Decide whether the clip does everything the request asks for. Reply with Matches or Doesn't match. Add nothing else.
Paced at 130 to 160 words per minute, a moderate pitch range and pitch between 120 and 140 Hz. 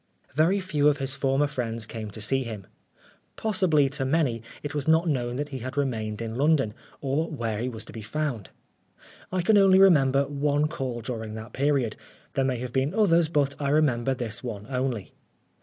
Doesn't match